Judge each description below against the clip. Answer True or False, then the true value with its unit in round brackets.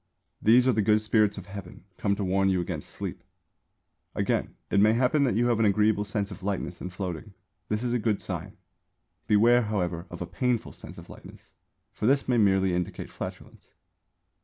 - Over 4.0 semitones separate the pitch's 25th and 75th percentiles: False (3.0 semitones)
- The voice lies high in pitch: False (105 Hz)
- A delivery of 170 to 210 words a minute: True (190 wpm)